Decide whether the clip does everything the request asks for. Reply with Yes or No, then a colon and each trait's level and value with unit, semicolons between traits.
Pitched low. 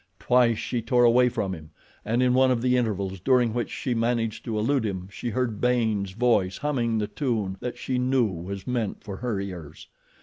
Yes: low, 115 Hz